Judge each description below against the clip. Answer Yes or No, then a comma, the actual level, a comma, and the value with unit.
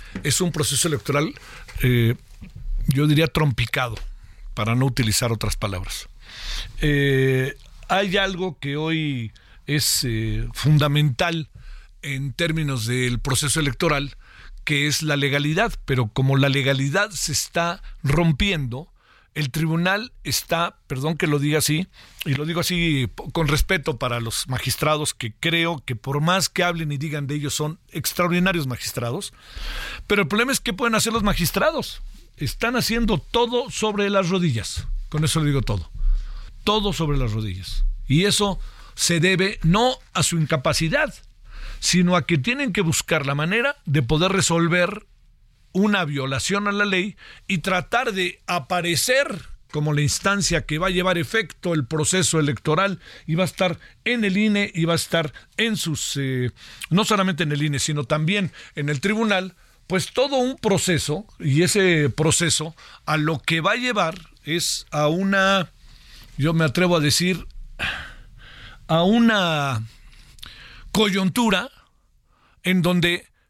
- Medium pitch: Yes, medium, 160 Hz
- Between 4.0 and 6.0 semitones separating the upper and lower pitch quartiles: Yes, average, 5.1 semitones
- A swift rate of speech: No, average, 150 wpm